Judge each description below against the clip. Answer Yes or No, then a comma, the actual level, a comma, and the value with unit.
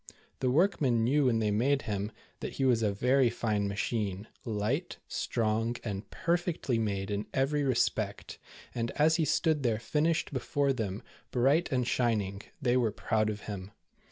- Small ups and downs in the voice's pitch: No, average, 4.5 semitones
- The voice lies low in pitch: Yes, low, 120 Hz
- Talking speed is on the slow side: No, average, 165 wpm